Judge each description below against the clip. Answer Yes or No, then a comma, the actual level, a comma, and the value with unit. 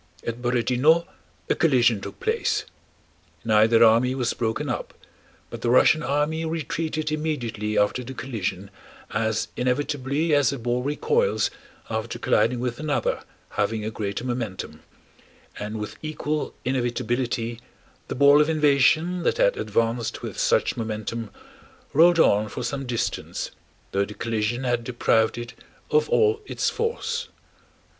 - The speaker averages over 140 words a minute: No, slow, 135 wpm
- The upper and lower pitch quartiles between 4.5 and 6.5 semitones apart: Yes, average, 5.0 semitones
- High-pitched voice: No, low, 125 Hz